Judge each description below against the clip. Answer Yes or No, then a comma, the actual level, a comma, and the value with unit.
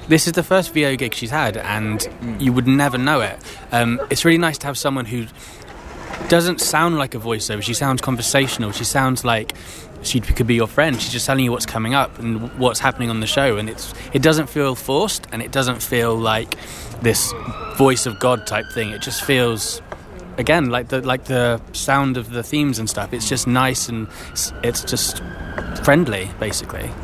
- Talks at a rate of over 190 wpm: Yes, average, 200 wpm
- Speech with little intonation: No, average, 3.5 semitones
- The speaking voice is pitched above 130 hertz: No, low, 125 Hz